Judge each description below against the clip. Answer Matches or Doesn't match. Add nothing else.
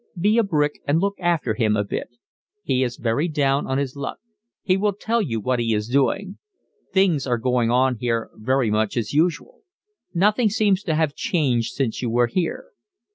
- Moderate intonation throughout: Doesn't match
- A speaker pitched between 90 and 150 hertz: Matches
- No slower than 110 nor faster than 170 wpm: Doesn't match